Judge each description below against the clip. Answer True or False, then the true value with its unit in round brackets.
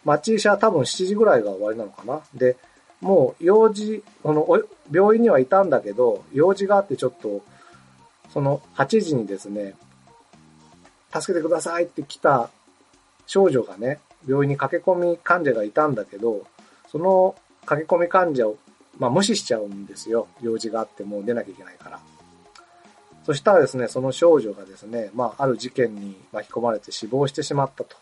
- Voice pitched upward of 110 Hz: True (135 Hz)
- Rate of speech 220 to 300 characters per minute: False (340 characters per minute)